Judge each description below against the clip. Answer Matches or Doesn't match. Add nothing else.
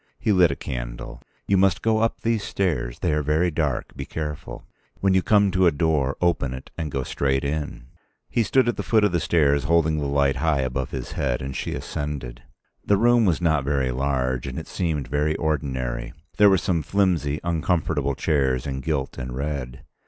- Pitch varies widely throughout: Doesn't match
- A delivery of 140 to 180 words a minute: Doesn't match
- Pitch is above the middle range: Doesn't match